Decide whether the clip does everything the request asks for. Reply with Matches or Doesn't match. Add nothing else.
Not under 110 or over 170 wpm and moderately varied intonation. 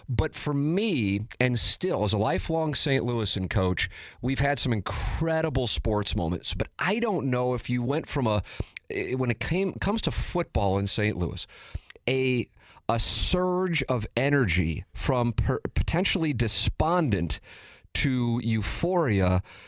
Doesn't match